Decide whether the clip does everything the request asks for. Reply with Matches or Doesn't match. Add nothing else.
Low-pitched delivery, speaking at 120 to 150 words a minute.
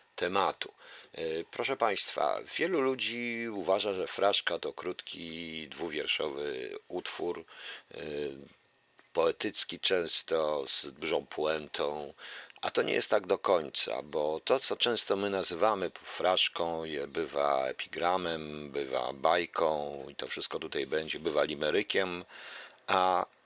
Doesn't match